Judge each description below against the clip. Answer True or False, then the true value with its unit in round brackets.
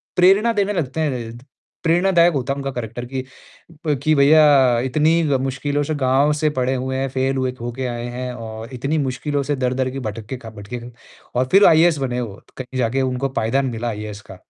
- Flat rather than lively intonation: False (3.2 semitones)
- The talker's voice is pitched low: True (130 Hz)